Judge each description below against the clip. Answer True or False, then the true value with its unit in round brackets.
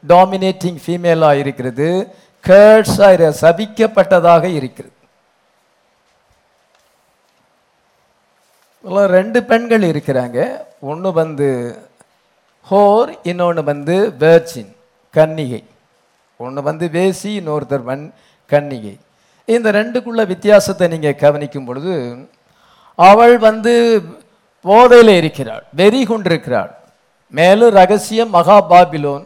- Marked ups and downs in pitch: True (6.0 semitones)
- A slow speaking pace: True (75 wpm)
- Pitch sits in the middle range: True (175 Hz)